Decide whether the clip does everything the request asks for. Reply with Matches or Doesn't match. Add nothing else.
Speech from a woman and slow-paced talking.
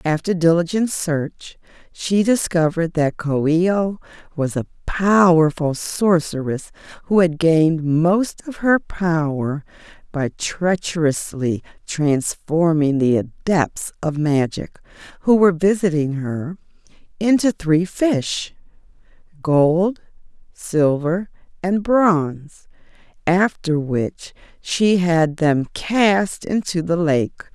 Matches